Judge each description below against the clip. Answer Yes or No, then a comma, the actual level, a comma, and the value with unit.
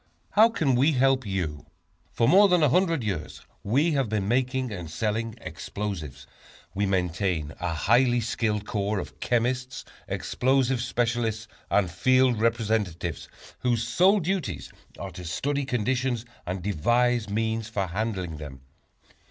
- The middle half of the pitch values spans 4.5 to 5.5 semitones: Yes, average, 5.0 semitones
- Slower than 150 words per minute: Yes, slow, 135 wpm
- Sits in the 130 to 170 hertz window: No, low, 115 Hz